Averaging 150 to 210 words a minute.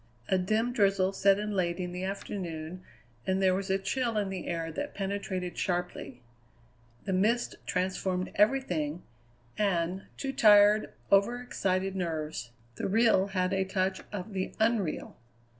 No: average, 140 wpm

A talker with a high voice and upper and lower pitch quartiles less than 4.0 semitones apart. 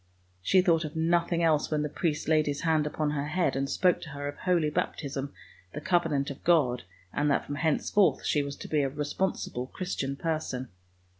No: medium, 150 Hz; narrow, 2.6 semitones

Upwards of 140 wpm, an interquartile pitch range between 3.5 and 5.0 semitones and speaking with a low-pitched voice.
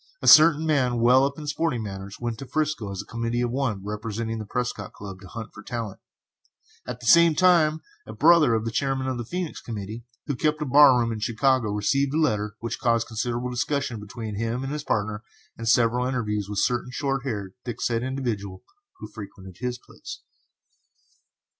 Yes: average, 195 wpm; average, 4.1 semitones; low, 120 Hz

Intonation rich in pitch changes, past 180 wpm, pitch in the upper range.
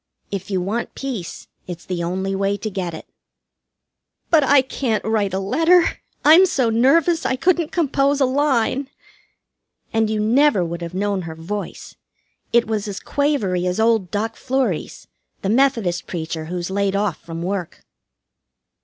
No: wide, 6.5 semitones; average, 155 wpm; high, 210 Hz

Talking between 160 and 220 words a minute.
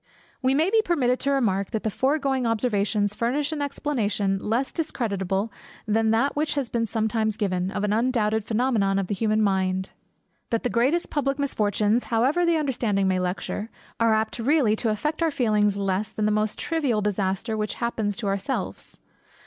Yes: average, 175 wpm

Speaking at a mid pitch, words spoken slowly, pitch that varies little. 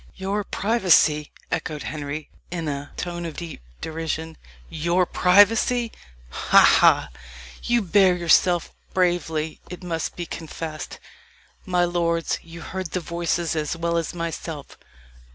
Yes: medium, 170 Hz; slow, 125 wpm; narrow, 2.1 semitones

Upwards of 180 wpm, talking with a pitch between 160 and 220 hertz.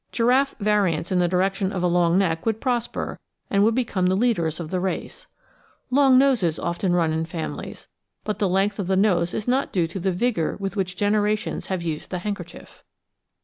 Yes: average, 195 wpm; high, 190 Hz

